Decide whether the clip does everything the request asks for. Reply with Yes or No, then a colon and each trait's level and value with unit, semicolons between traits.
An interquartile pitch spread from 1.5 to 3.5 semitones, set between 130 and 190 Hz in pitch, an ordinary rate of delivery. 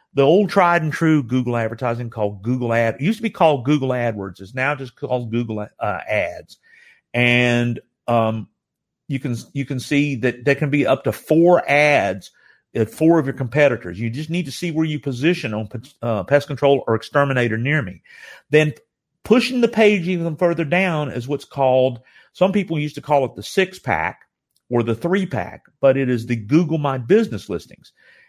No: average, 5.0 semitones; medium, 140 Hz; average, 195 wpm